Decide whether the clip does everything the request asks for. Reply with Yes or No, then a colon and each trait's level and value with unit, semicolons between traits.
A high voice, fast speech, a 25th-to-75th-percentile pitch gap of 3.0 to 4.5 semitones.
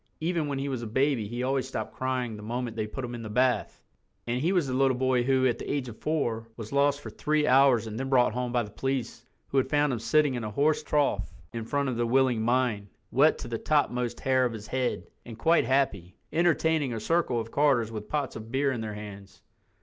No: low, 125 Hz; fast, 240 wpm; average, 3.4 semitones